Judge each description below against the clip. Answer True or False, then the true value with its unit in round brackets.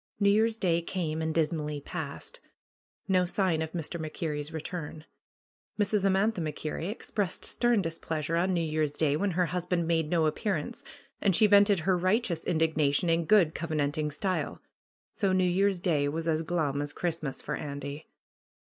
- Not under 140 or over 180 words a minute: True (165 wpm)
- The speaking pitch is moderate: True (165 Hz)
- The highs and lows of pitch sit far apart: False (3.4 semitones)